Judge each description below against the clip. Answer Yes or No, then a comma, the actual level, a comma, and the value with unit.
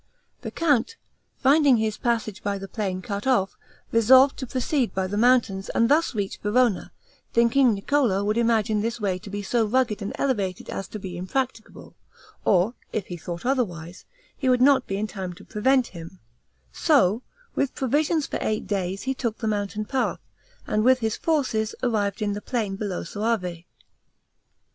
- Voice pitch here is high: Yes, high, 220 Hz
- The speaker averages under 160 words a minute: No, average, 170 wpm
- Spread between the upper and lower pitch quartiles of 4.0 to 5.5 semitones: Yes, average, 4.5 semitones